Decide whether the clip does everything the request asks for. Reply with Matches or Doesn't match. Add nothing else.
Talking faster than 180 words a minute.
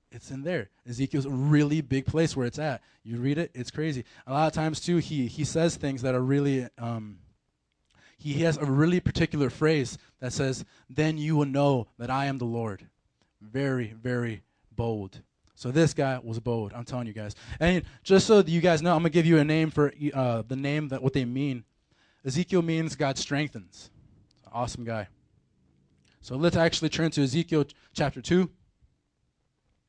Matches